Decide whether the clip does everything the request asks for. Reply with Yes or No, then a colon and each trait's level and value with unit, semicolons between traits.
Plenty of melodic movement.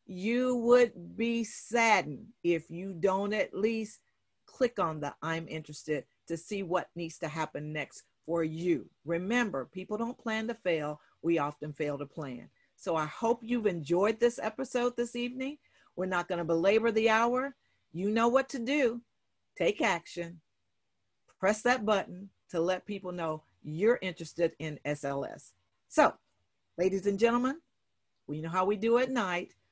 Yes: wide, 6.3 semitones